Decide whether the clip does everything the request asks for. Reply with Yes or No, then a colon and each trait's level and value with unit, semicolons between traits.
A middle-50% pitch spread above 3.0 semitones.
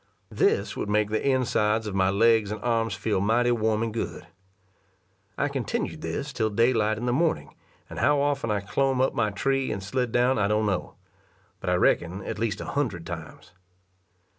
Yes: average, 3.8 semitones